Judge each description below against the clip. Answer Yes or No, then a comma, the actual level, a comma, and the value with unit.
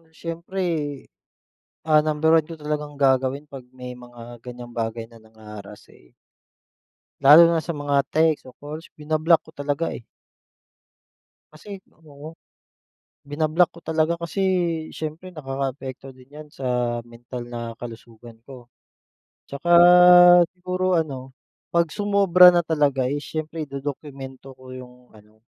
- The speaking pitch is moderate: Yes, medium, 145 Hz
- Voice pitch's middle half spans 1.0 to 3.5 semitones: No, average, 4.2 semitones